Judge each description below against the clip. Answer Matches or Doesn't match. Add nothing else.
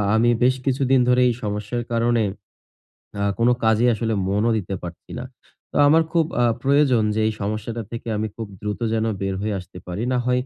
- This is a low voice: Matches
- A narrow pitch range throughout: Doesn't match